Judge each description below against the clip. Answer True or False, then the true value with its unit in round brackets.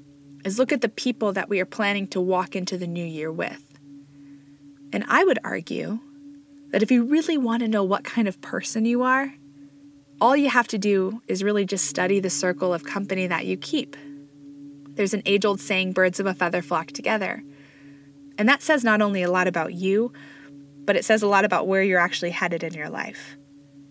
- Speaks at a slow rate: False (205 wpm)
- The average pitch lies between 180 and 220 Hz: True (185 Hz)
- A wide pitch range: True (6.9 semitones)